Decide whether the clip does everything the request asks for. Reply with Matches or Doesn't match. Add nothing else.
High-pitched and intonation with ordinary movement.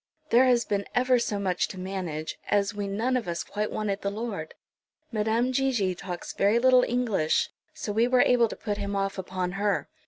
Matches